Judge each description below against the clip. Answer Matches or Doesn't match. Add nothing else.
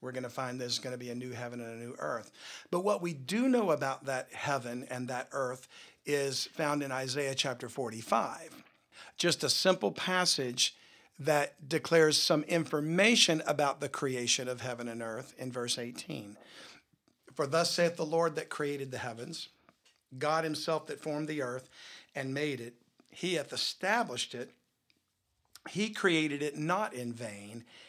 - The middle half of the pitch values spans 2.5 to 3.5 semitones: Doesn't match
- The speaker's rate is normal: Matches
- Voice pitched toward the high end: Doesn't match